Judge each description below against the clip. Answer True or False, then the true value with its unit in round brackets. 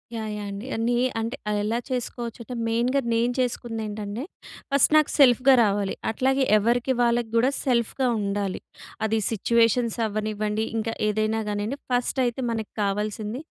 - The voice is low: False (230 Hz)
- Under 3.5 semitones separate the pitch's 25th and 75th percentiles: True (2.5 semitones)